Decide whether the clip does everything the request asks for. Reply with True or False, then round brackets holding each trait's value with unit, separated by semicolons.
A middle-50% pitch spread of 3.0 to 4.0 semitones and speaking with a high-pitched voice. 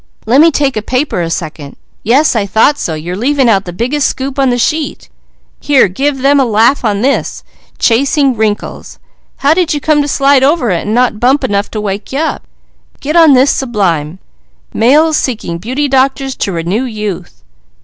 False (5.4 semitones; 255 Hz)